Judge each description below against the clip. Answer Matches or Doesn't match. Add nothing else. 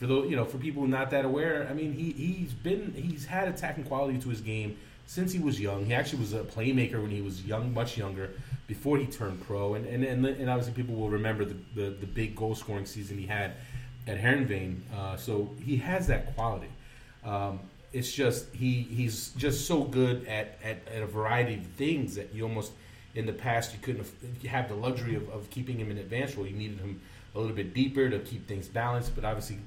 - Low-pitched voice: Matches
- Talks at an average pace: Doesn't match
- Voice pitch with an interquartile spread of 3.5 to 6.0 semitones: Matches